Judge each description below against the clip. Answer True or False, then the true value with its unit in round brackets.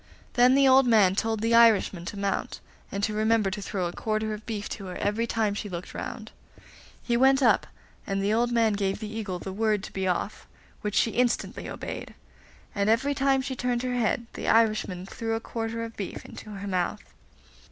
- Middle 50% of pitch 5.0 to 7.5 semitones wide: False (2.7 semitones)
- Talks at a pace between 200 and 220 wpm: True (205 wpm)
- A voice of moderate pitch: False (220 Hz)